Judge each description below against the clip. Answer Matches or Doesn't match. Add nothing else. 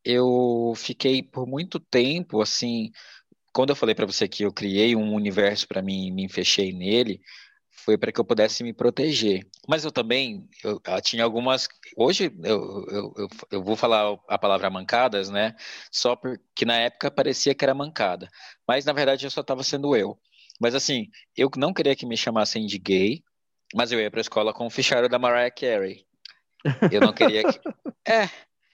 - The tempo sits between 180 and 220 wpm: Matches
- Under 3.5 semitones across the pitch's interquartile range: Doesn't match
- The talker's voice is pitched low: Matches